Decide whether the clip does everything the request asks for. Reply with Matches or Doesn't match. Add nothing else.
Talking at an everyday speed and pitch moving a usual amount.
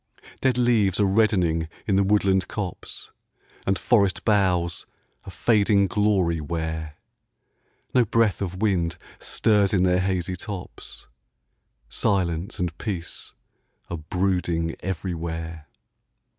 Doesn't match